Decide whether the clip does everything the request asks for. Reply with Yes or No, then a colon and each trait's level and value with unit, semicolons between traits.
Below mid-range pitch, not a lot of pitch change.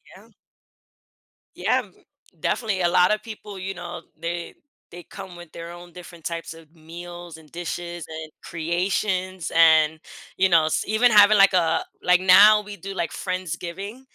No: medium, 175 Hz; narrow, 2.3 semitones